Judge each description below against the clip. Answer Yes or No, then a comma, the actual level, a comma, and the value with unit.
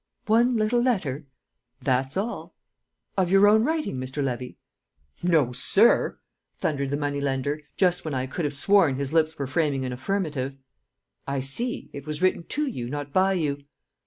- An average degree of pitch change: No, wide, 6.1 semitones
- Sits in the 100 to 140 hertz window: No, medium, 150 Hz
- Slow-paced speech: No, average, 165 wpm